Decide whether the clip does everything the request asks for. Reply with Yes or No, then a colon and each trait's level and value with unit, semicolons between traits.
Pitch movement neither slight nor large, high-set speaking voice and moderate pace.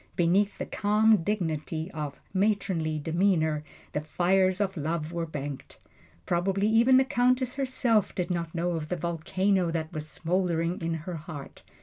No: average, 3.9 semitones; medium, 175 Hz; average, 150 wpm